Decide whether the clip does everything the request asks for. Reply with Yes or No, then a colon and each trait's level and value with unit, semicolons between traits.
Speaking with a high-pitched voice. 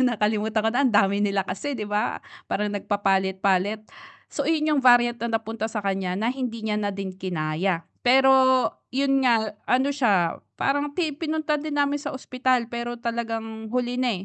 Yes: high, 225 Hz